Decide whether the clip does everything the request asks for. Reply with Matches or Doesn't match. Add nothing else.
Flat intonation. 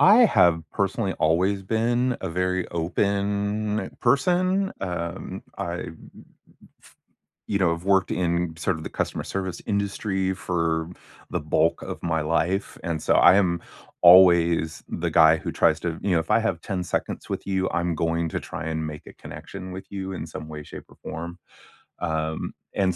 Doesn't match